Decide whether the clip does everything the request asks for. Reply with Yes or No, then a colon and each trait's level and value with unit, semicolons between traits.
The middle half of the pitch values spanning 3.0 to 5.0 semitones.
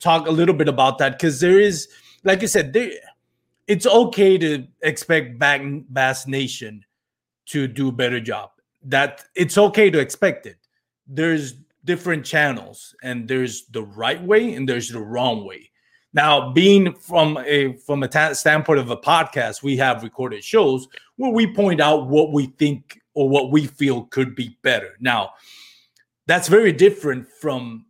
Yes: average, 4.3 semitones